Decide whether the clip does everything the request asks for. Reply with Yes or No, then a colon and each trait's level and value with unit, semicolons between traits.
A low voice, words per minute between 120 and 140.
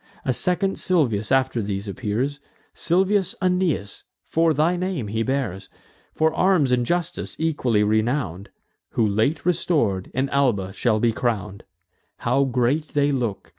Yes: low, 130 Hz; slow, 135 wpm